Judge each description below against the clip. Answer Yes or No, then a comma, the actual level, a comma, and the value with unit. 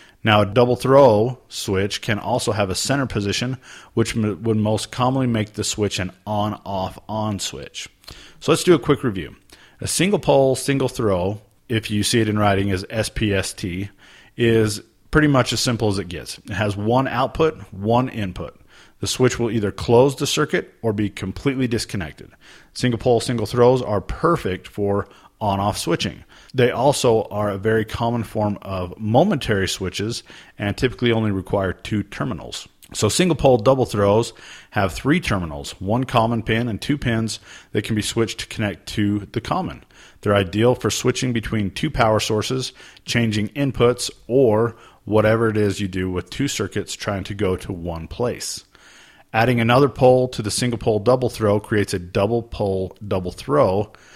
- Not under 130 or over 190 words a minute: Yes, average, 175 wpm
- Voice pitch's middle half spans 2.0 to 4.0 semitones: Yes, average, 3.5 semitones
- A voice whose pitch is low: Yes, low, 110 Hz